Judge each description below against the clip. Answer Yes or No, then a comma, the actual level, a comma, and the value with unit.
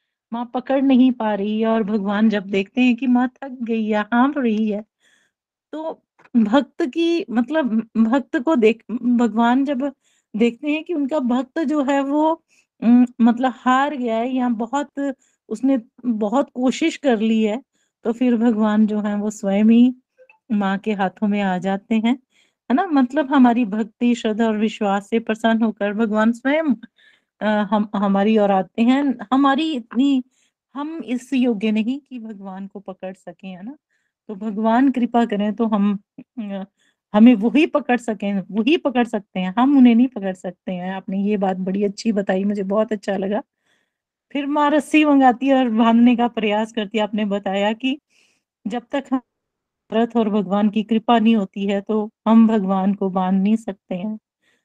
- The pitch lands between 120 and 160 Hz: No, high, 230 Hz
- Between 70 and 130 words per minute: No, average, 165 wpm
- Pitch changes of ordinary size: Yes, average, 3.7 semitones